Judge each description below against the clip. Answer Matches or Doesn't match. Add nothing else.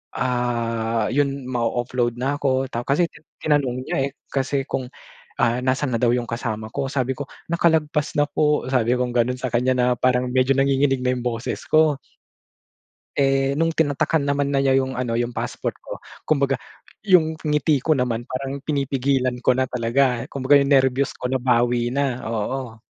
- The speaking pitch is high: Doesn't match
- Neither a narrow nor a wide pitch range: Doesn't match